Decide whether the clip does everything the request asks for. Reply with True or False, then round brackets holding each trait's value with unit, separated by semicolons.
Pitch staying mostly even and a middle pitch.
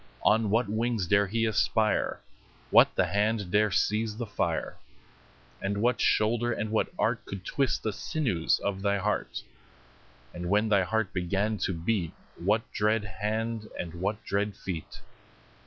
False (2.2 semitones; 105 Hz)